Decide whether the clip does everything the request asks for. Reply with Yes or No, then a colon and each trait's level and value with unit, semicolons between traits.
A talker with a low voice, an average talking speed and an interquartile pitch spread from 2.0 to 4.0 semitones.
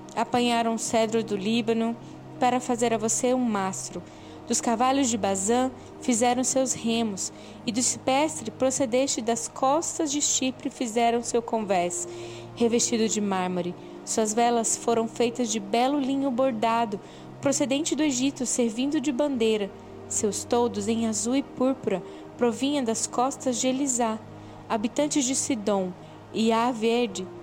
No: high, 240 Hz; average, 140 wpm; average, 2.7 semitones